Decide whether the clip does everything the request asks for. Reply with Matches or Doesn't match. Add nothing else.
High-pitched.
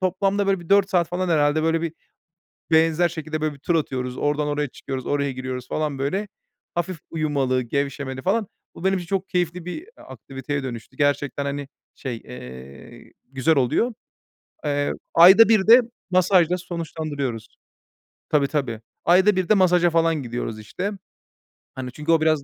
Doesn't match